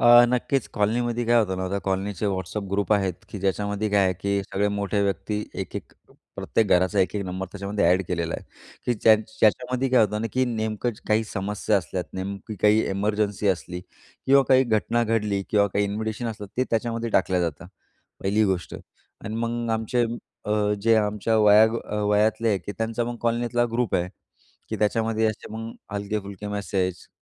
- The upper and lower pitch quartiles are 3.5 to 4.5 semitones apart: No, narrow, 2.4 semitones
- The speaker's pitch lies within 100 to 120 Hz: Yes, low, 105 Hz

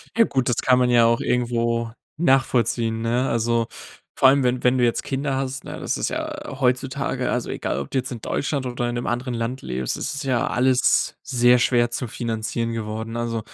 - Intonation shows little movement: Yes, narrow, 2.0 semitones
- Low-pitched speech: Yes, low, 120 Hz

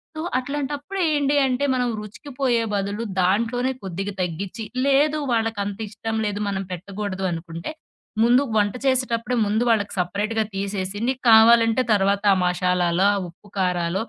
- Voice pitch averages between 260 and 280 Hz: No, high, 210 Hz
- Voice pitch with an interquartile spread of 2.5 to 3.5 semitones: No, average, 4.3 semitones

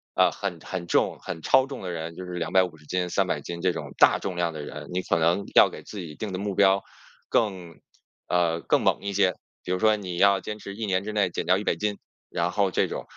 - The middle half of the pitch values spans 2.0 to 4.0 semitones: Yes, narrow, 2.6 semitones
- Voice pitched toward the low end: Yes, very low, 90 Hz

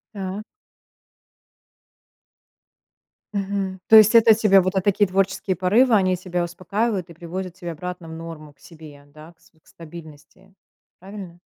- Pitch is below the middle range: No, medium, 185 Hz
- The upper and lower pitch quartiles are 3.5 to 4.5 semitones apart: No, average, 2.9 semitones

